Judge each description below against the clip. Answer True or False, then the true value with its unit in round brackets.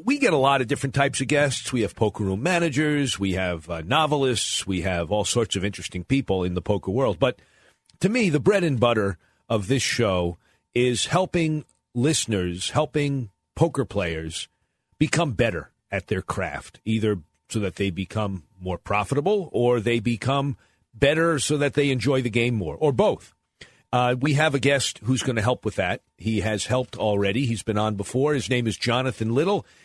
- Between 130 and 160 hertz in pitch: False (120 Hz)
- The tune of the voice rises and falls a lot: True (5.7 semitones)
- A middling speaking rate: True (190 wpm)